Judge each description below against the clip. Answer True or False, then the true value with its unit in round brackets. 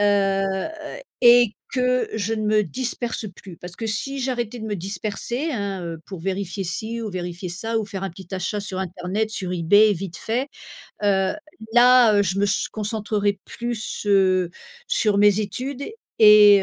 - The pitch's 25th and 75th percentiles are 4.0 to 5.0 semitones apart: False (2.8 semitones)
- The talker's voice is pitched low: False (205 Hz)